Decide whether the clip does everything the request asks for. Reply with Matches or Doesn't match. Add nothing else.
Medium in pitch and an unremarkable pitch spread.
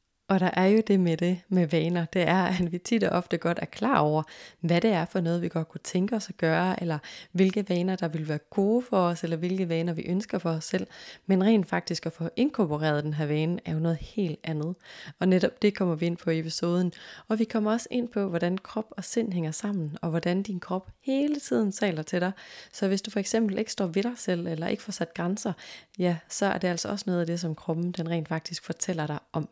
Matches